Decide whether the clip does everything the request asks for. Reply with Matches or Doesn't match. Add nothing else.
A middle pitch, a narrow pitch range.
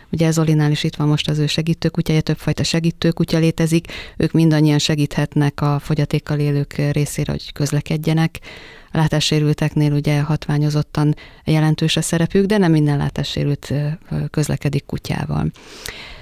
Matches